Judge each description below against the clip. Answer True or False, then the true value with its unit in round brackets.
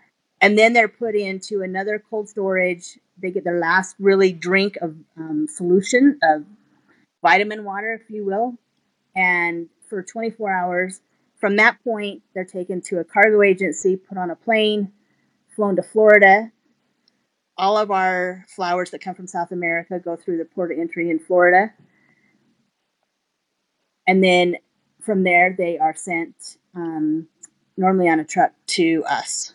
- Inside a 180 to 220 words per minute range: False (150 wpm)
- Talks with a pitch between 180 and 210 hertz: True (190 Hz)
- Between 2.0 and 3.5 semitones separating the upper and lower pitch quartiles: True (3.0 semitones)